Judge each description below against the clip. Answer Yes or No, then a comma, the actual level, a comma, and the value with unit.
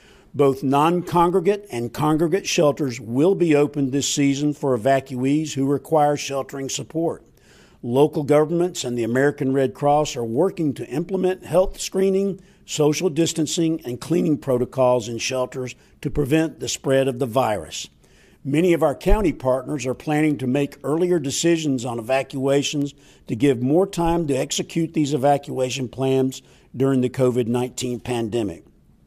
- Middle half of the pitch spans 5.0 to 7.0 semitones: No, average, 3.7 semitones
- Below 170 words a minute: Yes, average, 145 wpm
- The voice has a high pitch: No, medium, 140 Hz